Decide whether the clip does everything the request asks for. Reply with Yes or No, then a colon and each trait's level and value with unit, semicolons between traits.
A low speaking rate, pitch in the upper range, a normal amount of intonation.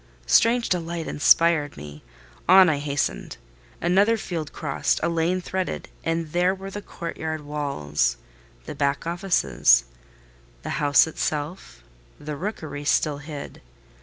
No: slow, 110 wpm; medium, 155 Hz; average, 3.8 semitones